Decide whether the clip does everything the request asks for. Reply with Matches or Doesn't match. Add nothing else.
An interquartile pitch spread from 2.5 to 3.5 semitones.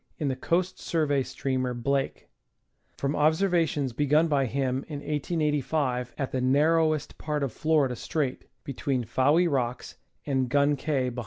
Matches